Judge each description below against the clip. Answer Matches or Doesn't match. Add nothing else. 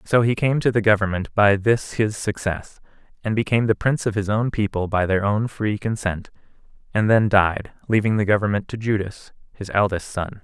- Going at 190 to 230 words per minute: Matches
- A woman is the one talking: Doesn't match